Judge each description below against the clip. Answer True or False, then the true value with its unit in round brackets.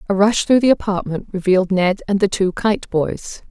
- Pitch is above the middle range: True (195 Hz)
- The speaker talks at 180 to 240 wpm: True (205 wpm)